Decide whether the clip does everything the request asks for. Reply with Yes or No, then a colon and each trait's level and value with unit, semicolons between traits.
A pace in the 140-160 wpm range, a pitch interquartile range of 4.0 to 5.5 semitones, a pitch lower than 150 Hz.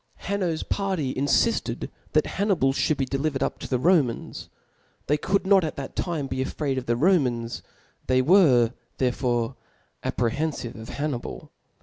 Yes: average, 150 wpm; average, 5.2 semitones; medium, 140 Hz